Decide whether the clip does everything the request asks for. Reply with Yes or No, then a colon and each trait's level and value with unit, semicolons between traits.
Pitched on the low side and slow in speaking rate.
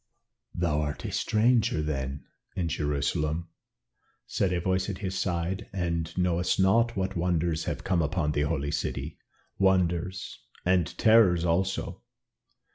Yes: very low, 90 Hz; slow, 130 wpm